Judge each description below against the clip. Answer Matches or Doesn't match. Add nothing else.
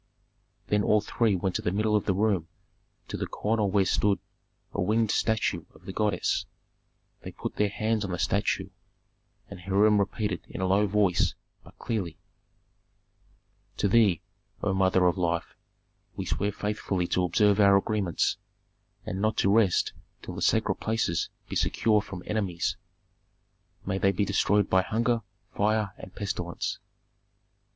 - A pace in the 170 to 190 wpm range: Doesn't match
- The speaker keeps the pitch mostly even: Matches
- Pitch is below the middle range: Matches